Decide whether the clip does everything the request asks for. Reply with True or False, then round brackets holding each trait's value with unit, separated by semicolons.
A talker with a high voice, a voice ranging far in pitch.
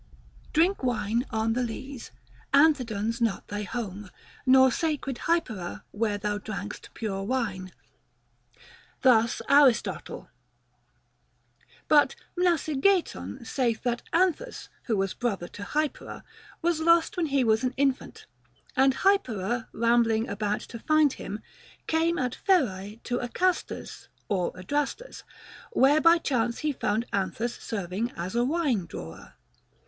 True (240 Hz; 5.8 semitones)